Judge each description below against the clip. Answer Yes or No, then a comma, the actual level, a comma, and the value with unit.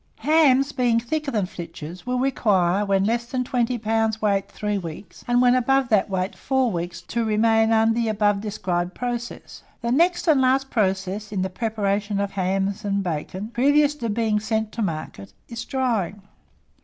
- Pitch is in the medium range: No, high, 220 Hz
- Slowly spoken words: No, average, 175 wpm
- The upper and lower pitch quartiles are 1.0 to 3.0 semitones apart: No, average, 3.9 semitones